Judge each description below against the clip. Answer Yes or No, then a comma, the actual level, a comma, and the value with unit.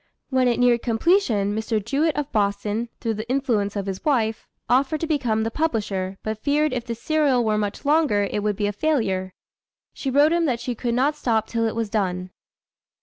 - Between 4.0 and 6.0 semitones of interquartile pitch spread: Yes, average, 4.9 semitones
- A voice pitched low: No, high, 230 Hz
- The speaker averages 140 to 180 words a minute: No, fast, 205 wpm